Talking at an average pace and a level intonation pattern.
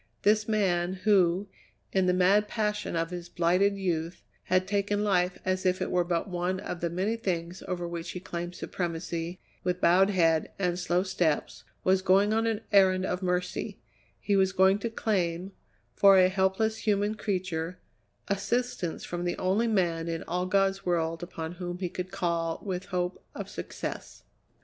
Yes: average, 170 wpm; narrow, 2.1 semitones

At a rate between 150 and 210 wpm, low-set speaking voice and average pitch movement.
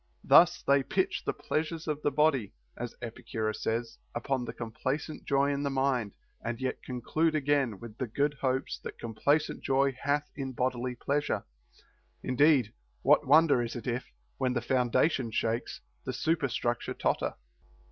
Yes: average, 155 wpm; low, 130 Hz; average, 3.2 semitones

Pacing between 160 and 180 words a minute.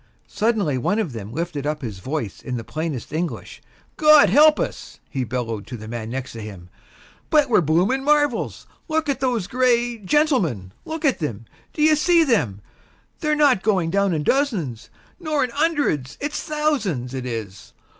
Yes: average, 170 wpm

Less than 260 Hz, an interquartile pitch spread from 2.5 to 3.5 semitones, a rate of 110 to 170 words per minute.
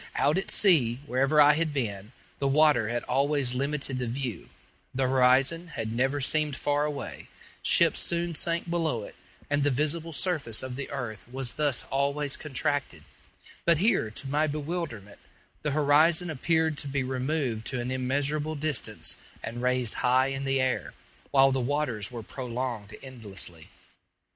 Yes: low, 135 Hz; average, 3.2 semitones; average, 160 wpm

